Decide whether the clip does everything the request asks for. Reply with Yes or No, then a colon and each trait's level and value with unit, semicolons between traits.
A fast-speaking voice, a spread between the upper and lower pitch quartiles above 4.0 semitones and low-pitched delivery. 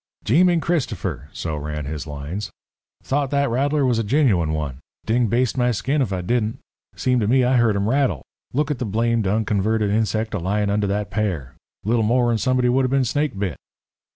Yes: fast, 210 wpm; average, 4.6 semitones; low, 110 Hz